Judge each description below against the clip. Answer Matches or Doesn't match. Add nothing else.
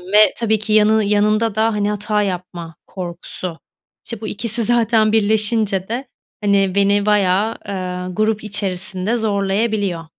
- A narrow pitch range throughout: Matches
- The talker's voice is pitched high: Matches